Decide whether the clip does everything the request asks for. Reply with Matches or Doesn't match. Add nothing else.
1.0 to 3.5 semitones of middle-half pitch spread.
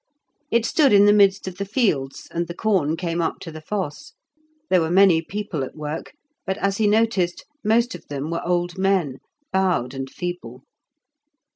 Doesn't match